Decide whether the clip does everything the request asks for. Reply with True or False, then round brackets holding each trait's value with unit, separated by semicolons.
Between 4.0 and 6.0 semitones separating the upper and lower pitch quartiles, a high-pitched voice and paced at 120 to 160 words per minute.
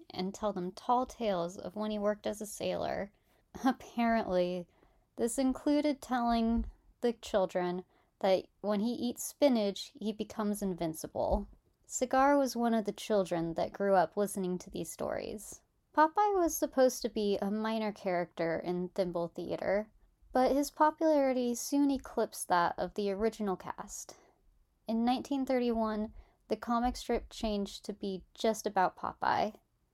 True (4.6 semitones; 215 Hz; 140 wpm)